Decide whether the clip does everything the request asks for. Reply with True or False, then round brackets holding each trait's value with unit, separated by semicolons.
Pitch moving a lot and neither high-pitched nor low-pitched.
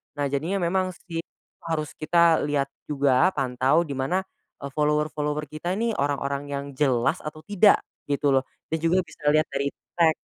False (3.2 semitones; 150 Hz)